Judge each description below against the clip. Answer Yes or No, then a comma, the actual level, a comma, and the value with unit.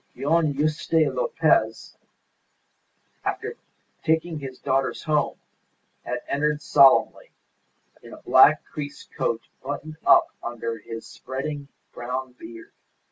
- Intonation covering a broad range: No, average, 3.5 semitones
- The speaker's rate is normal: No, slow, 105 wpm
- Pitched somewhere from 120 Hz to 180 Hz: Yes, medium, 140 Hz